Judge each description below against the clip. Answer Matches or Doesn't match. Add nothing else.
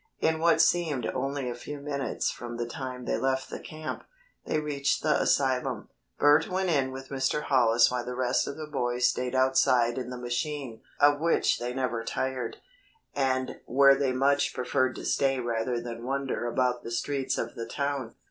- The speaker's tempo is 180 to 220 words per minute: Matches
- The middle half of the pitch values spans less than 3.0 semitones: Matches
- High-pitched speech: Doesn't match